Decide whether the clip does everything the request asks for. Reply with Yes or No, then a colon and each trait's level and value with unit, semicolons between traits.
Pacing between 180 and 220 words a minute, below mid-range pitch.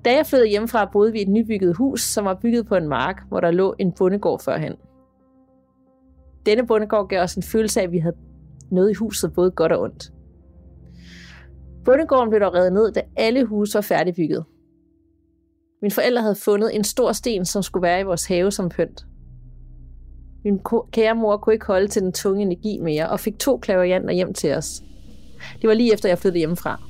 No: average, 200 wpm; medium, 185 Hz